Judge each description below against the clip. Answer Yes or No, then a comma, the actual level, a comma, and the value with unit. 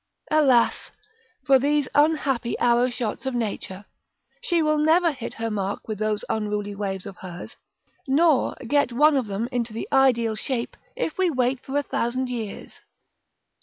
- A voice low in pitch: No, high, 245 Hz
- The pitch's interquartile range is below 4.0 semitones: No, average, 4.9 semitones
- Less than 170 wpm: Yes, average, 160 wpm